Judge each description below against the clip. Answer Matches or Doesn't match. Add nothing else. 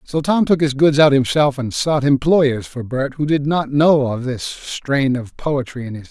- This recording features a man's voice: Matches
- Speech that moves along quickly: Matches